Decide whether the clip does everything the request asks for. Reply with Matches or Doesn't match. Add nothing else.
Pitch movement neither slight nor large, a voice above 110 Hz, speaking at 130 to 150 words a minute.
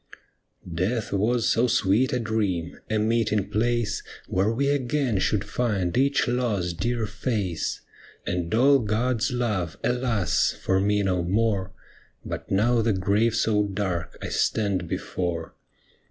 Doesn't match